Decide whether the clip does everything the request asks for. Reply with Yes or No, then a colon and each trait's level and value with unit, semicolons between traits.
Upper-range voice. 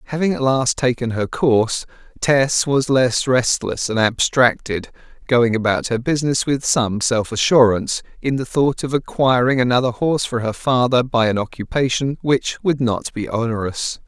No: low, 125 Hz